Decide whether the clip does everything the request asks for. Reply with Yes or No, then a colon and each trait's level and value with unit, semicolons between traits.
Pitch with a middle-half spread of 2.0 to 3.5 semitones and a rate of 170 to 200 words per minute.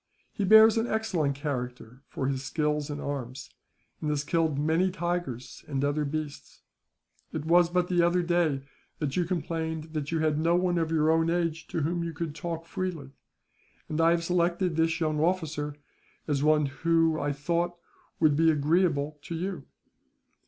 Yes: average, 2.8 semitones; average, 175 wpm